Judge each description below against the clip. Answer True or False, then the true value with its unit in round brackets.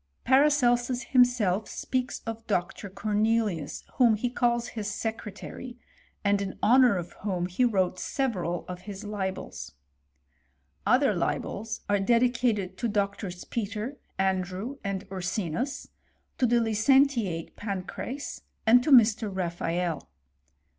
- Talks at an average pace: False (120 wpm)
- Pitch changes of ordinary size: True (4.2 semitones)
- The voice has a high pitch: True (215 Hz)